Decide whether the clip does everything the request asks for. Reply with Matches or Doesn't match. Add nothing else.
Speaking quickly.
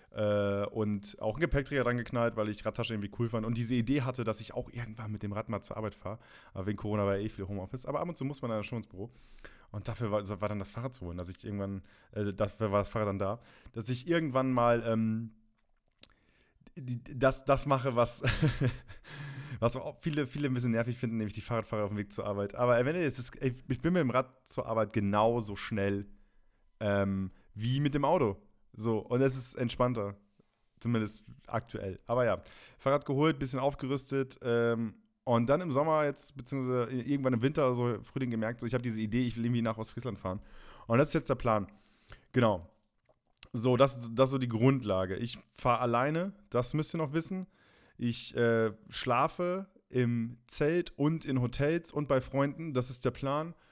Matches